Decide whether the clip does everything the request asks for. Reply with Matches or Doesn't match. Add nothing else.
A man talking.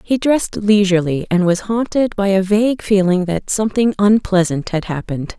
Doesn't match